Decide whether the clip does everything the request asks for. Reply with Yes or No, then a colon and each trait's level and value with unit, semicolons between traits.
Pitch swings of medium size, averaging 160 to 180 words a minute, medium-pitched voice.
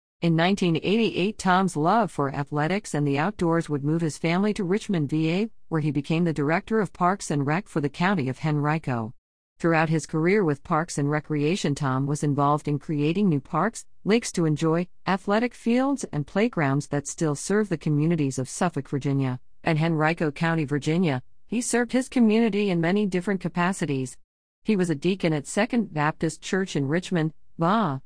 Yes: average, 4.5 semitones; average, 175 wpm; medium, 165 Hz